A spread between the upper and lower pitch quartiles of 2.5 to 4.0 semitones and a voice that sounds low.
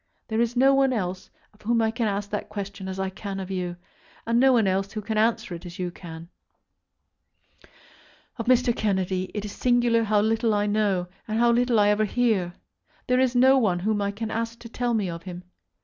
No: average, 3.5 semitones; high, 215 Hz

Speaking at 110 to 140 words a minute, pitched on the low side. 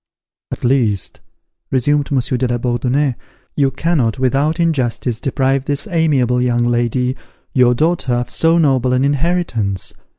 Yes: slow, 135 wpm; low, 130 Hz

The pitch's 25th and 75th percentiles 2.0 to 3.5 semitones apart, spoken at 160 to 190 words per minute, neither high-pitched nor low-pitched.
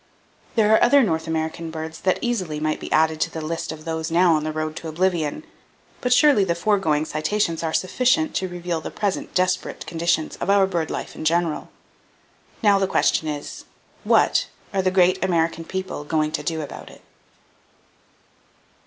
Yes: average, 3.1 semitones; average, 180 wpm; medium, 170 Hz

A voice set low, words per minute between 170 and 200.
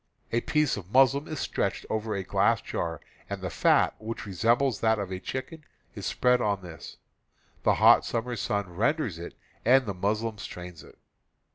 Yes: low, 110 Hz; average, 180 wpm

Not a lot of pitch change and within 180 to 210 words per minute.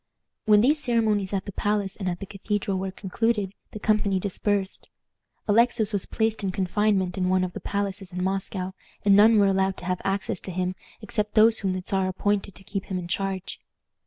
Yes: narrow, 1.9 semitones; average, 200 wpm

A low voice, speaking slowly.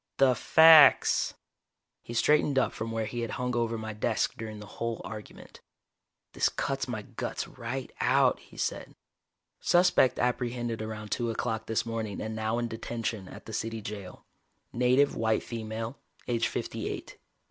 No: low, 115 Hz; average, 160 wpm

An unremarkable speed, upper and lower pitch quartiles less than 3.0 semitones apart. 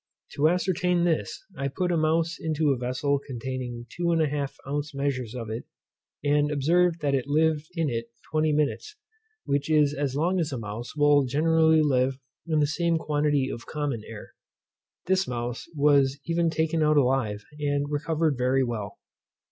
No: average, 165 wpm; average, 3.3 semitones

